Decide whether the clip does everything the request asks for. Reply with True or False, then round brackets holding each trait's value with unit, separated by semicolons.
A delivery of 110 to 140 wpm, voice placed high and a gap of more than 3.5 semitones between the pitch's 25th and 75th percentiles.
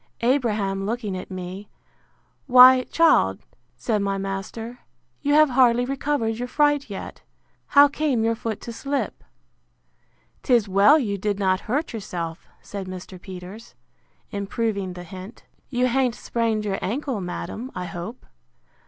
True (135 wpm; 220 Hz; 4.6 semitones)